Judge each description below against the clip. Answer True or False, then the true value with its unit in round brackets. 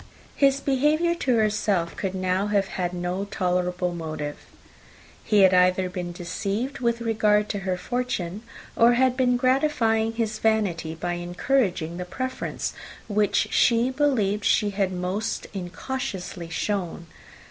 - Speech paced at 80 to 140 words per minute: True (135 wpm)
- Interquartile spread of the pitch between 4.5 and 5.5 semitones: True (4.8 semitones)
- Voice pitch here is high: True (205 Hz)